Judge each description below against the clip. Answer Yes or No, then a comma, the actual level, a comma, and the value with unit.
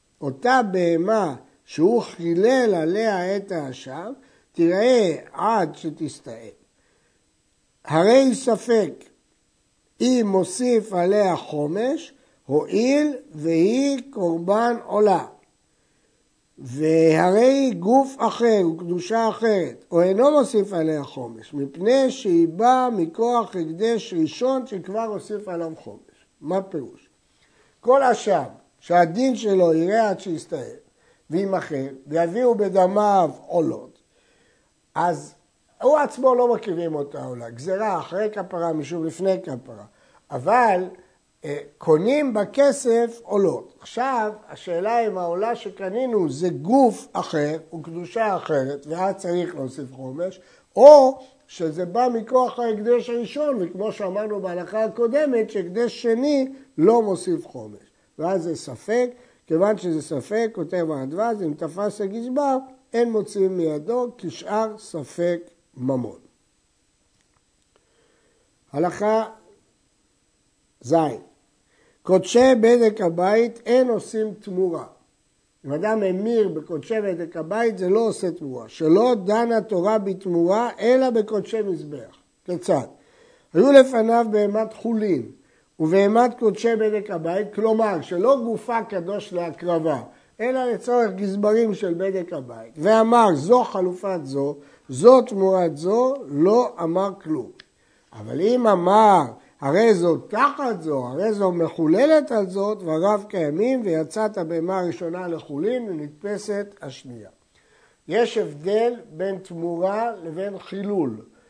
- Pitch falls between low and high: No, high, 200 Hz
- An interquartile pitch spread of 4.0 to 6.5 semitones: Yes, wide, 5.5 semitones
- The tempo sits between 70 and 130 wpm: Yes, average, 105 wpm